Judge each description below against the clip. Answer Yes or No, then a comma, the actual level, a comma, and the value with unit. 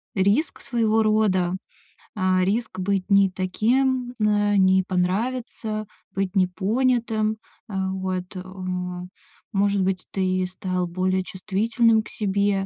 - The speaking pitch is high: Yes, high, 200 Hz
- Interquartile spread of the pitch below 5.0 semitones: Yes, average, 2.8 semitones